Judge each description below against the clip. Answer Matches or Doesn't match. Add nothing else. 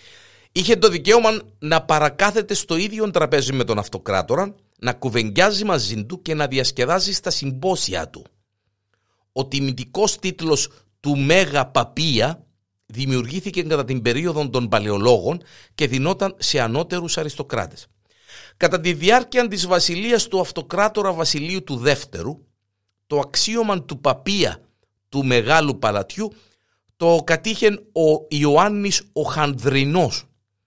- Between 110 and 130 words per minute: Matches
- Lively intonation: Matches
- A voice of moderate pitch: Matches